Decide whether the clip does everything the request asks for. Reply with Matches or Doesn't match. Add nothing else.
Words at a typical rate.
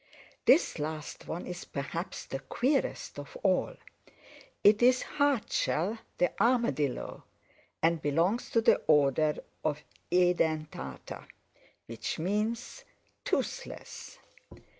Doesn't match